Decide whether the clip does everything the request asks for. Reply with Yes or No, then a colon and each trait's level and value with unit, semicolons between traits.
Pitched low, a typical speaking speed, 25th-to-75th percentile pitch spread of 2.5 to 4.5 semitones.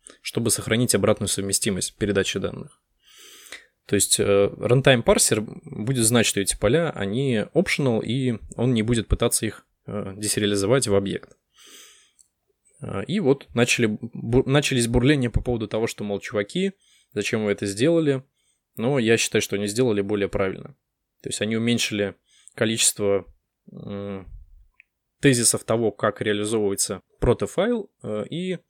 Yes: low, 110 Hz; average, 140 wpm; average, 3.9 semitones